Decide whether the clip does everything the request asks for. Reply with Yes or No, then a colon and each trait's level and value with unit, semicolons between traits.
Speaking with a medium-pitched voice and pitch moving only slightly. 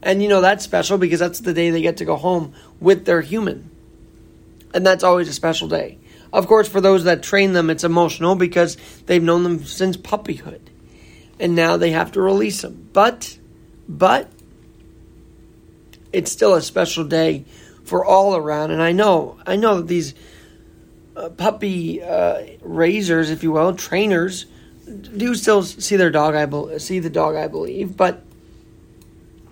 No: medium, 175 Hz; average, 3.0 semitones